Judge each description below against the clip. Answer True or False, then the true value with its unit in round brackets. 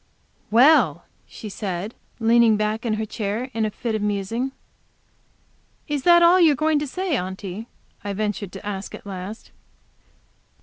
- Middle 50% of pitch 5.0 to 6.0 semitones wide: False (4.3 semitones)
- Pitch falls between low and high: False (220 Hz)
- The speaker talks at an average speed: True (165 wpm)